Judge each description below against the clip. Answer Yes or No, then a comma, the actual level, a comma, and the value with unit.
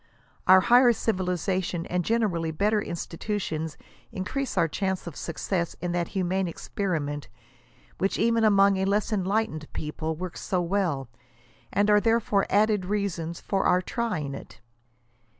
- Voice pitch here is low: No, high, 190 Hz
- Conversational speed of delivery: Yes, average, 145 wpm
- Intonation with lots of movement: No, average, 3.6 semitones